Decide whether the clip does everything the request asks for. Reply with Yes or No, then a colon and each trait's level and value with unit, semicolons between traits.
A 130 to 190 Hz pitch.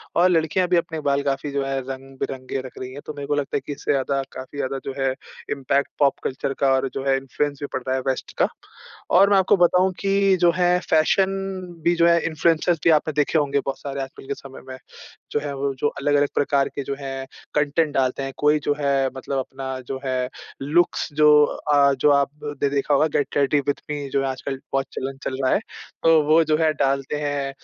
Yes: medium, 140 Hz